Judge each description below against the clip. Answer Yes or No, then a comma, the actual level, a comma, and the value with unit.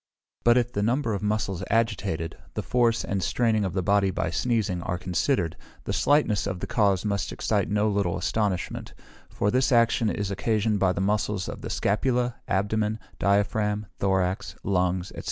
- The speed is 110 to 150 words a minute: No, average, 170 wpm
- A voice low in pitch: Yes, low, 105 Hz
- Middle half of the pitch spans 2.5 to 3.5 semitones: Yes, average, 2.9 semitones